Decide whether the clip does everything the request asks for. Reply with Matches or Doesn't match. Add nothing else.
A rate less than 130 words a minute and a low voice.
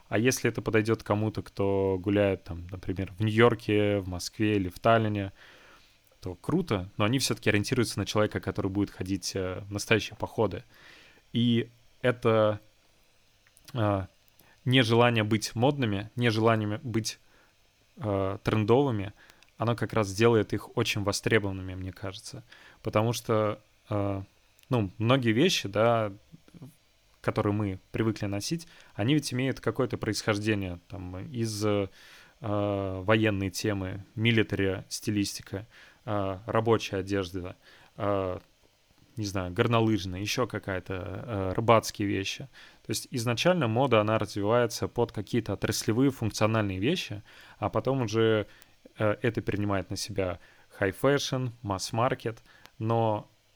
Matches